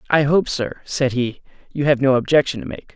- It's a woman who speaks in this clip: No, male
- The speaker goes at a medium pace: No, fast, 225 wpm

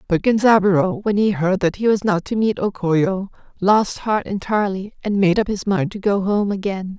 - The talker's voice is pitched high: Yes, high, 200 Hz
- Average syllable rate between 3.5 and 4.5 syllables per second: No, 5.0 syllables/s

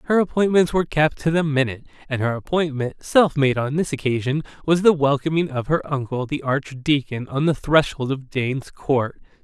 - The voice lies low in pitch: No, medium, 145 Hz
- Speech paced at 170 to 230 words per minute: Yes, average, 185 wpm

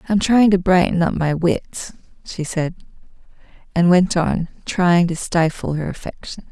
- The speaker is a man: No, female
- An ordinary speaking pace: Yes, average, 155 wpm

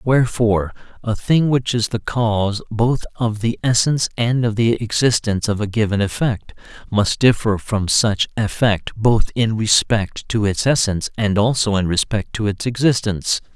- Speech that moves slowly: No, average, 165 wpm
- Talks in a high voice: No, low, 110 Hz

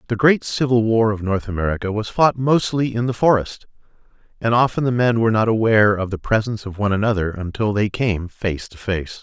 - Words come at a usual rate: No, fast, 210 wpm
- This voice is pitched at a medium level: No, low, 110 Hz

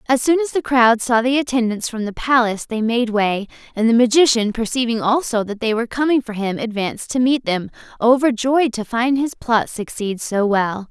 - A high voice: Yes, high, 235 Hz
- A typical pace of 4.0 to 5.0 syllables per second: No, 5.2 syllables/s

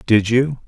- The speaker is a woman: No, male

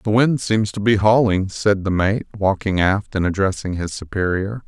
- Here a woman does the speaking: No, male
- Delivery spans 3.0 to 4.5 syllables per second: No, 4.7 syllables/s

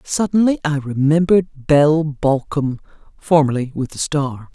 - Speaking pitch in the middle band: Yes, medium, 150 Hz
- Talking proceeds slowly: Yes, slow, 120 wpm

